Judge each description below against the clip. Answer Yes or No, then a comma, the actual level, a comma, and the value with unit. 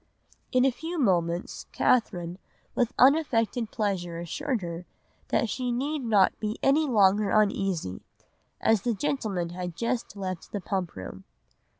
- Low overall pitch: No, high, 210 Hz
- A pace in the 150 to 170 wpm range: No, slow, 135 wpm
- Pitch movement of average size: No, wide, 5.8 semitones